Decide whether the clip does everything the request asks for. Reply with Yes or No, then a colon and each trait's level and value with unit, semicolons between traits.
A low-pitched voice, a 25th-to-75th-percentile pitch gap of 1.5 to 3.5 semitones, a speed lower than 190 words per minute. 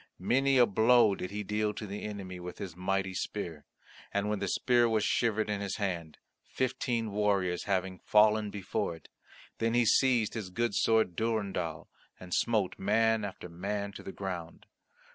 Yes: low, 105 Hz; average, 3.0 semitones; average, 170 wpm